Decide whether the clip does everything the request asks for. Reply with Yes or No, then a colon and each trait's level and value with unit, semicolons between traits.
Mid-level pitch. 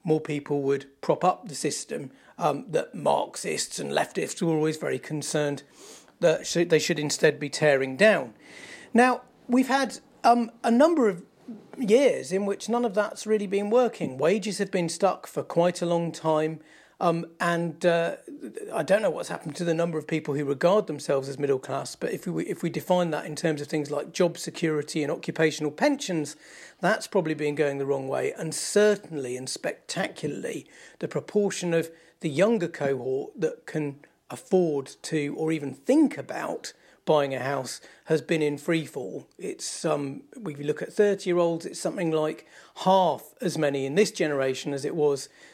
Yes: medium, 165 Hz